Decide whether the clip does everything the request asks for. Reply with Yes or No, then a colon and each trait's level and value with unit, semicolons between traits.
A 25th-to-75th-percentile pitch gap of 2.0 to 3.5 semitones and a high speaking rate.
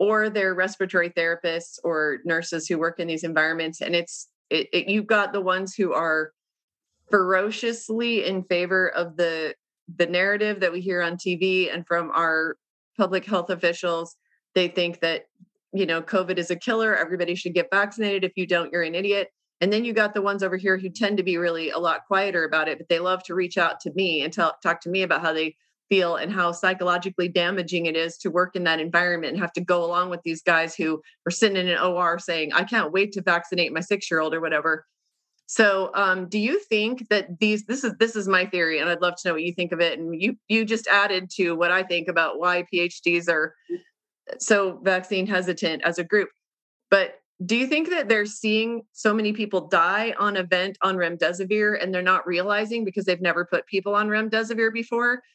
Yes: average, 3.1 semitones; fast, 215 wpm